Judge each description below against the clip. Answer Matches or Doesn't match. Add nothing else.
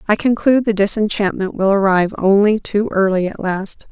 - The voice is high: Matches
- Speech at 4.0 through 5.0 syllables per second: Doesn't match